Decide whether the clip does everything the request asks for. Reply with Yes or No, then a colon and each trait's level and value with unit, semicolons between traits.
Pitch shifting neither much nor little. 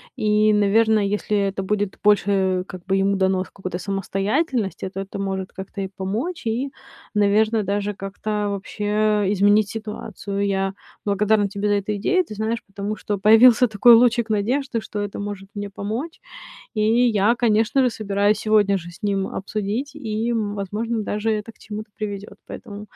No: narrow, 1.8 semitones